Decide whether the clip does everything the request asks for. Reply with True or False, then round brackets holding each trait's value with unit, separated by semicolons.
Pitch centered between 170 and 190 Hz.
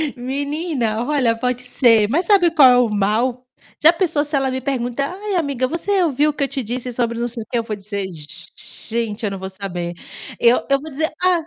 False (250 Hz)